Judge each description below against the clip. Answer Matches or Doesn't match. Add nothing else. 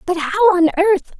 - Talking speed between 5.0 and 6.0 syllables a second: Doesn't match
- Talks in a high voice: Matches